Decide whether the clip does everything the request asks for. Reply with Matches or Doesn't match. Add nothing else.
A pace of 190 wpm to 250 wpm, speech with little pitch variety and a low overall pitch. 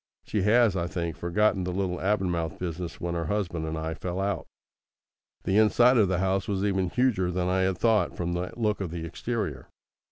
Doesn't match